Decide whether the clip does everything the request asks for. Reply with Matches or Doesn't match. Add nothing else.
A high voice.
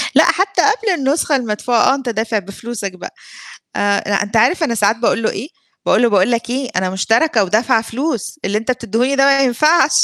Matches